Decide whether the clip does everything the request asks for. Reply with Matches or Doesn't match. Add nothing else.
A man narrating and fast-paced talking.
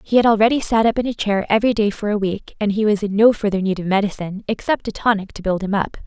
Doesn't match